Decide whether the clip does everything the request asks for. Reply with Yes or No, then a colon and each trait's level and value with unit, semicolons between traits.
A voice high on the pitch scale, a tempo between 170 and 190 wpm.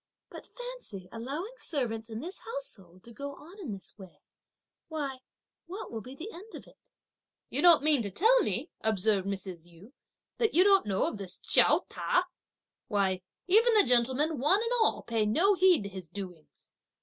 Yes: very high, 260 Hz; average, 175 wpm